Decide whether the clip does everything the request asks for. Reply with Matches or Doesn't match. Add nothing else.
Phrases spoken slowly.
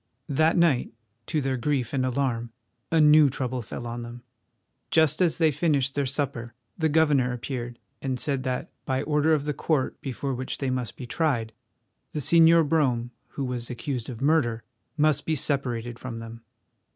Doesn't match